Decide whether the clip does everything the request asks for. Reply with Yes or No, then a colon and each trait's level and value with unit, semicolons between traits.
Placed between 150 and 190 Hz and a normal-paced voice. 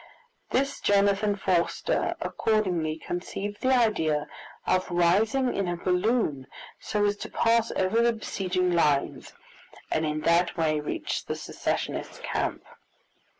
No: medium, 185 Hz; slow, 125 wpm